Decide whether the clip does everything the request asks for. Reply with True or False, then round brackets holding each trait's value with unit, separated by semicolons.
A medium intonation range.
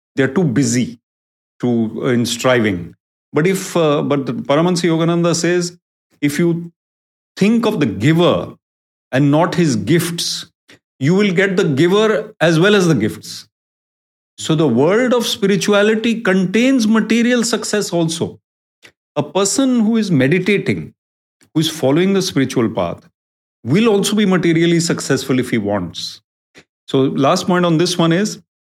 False (7.1 semitones)